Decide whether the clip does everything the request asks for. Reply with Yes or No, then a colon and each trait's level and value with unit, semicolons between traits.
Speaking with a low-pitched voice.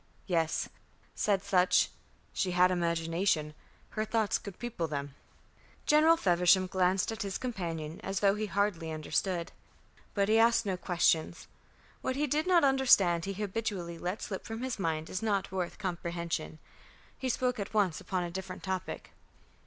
No: high, 190 Hz